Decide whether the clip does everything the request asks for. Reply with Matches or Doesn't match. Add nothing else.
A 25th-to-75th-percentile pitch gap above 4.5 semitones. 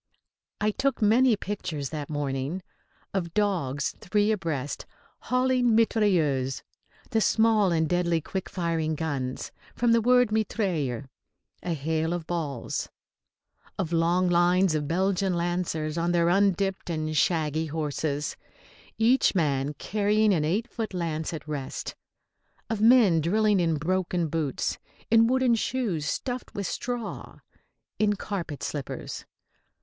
Matches